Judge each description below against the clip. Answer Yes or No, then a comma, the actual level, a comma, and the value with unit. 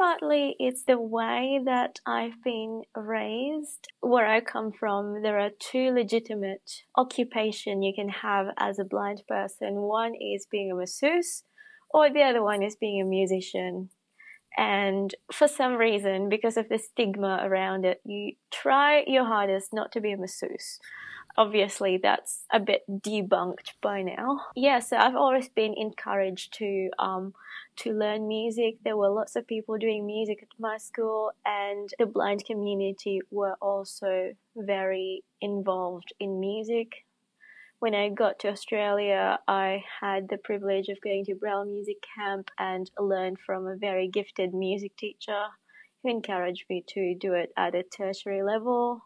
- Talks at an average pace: Yes, average, 155 wpm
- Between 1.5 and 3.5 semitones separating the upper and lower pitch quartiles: Yes, average, 2.8 semitones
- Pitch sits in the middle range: No, high, 210 Hz